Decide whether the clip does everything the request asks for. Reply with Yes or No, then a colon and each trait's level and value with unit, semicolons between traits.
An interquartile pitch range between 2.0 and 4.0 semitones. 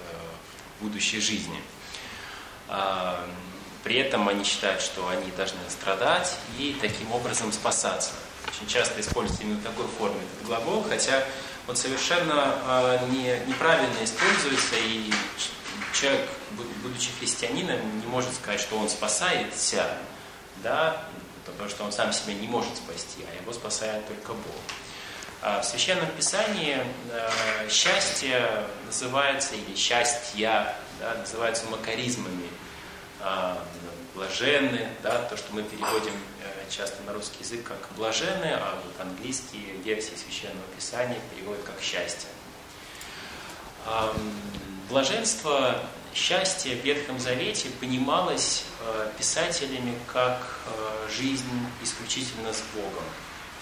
Yes: average, 3.7 semitones